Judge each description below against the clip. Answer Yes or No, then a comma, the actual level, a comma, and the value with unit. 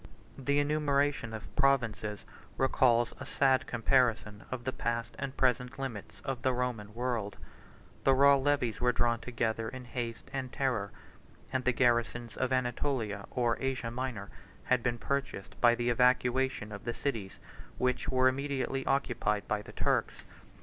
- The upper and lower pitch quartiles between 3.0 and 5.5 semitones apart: No, narrow, 2.4 semitones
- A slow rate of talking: No, average, 150 wpm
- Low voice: Yes, low, 125 Hz